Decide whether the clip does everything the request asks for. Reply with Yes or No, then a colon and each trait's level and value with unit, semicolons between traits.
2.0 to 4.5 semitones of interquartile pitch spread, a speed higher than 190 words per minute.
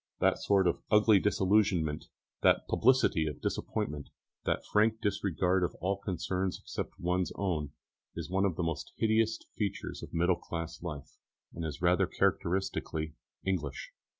No: average, 3.2 semitones; average, 150 wpm